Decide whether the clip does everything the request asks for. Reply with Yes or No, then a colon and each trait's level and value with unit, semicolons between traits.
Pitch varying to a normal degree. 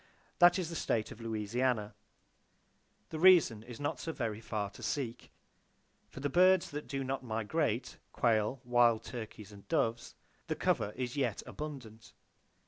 Yes: average, 4.7 semitones